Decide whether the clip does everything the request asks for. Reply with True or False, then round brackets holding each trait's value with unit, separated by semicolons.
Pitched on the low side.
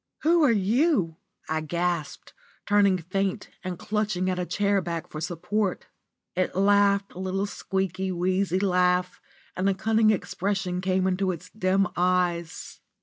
False (185 Hz)